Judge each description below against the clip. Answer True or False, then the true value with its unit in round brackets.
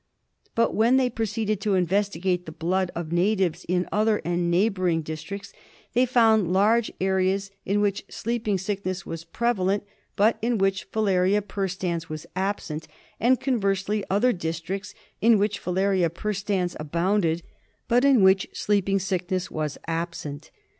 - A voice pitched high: True (195 Hz)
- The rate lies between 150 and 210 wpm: False (140 wpm)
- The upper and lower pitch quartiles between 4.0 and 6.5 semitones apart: False (3.1 semitones)